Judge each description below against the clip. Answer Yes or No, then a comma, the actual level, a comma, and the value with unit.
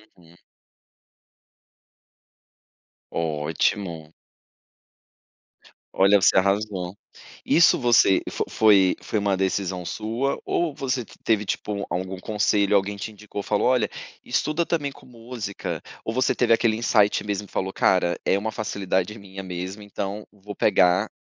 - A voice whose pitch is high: No, low, 100 Hz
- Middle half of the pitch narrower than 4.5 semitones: Yes, average, 2.7 semitones